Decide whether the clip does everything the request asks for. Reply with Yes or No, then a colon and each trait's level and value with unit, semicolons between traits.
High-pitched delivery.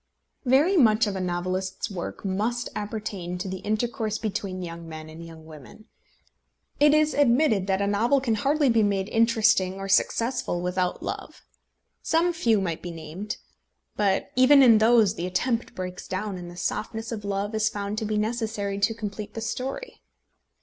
Yes: high, 210 Hz